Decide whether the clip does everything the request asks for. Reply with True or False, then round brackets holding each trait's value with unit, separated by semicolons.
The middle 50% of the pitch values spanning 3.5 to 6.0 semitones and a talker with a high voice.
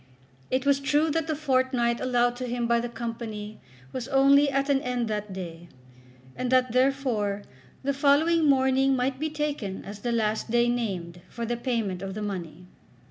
True (4.2 semitones; 245 Hz)